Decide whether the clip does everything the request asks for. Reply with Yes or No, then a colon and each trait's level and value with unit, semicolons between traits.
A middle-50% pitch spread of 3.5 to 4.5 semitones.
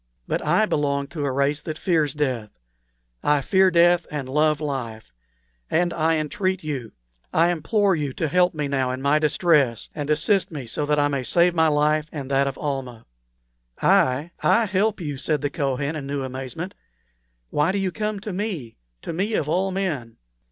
Yes: average, 4.0 semitones